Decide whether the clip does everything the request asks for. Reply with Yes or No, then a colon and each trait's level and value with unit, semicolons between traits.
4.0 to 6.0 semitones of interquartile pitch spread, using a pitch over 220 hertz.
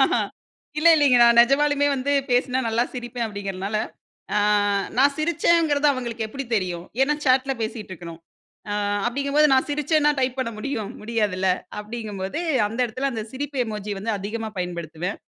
Yes: average, 4.9 semitones; high, 240 Hz